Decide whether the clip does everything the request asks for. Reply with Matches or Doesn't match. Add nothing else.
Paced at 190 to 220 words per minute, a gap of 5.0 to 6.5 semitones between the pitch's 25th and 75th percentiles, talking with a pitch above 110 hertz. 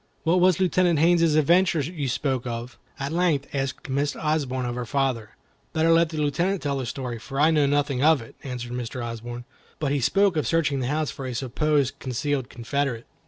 Doesn't match